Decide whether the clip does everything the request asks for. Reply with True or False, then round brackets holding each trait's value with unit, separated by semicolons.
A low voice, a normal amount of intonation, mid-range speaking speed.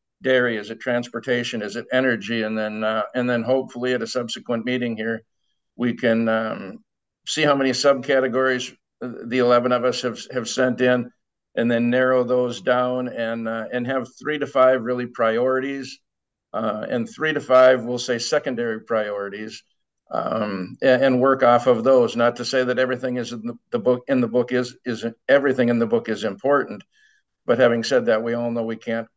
False (125 Hz; 1.8 semitones; 190 wpm)